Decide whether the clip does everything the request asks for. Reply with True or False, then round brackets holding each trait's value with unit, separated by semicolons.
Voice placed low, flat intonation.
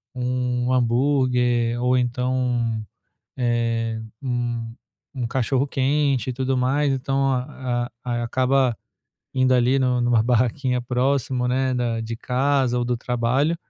True (125 Hz; 1.5 semitones)